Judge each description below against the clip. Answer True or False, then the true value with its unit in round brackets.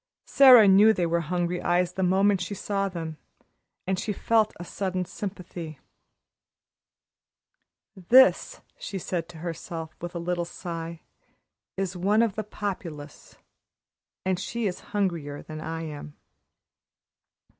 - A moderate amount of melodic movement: True (3.0 semitones)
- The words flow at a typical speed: False (130 wpm)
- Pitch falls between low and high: True (180 Hz)